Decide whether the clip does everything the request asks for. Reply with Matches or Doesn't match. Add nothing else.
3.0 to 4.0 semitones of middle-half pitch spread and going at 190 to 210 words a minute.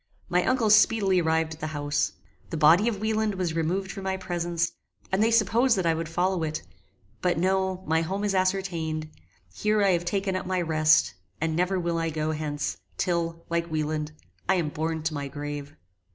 Matches